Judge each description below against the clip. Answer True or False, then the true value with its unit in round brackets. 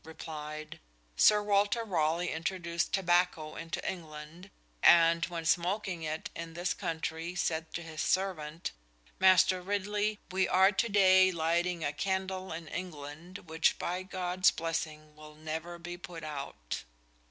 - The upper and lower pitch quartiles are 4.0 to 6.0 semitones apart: False (2.8 semitones)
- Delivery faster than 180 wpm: False (135 wpm)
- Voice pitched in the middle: True (170 Hz)